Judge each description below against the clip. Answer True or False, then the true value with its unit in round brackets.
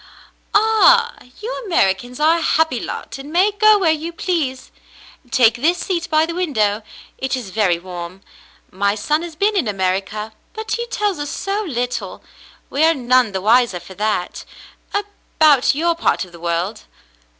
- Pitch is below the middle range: False (280 Hz)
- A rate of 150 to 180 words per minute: True (165 wpm)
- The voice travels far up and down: True (8.8 semitones)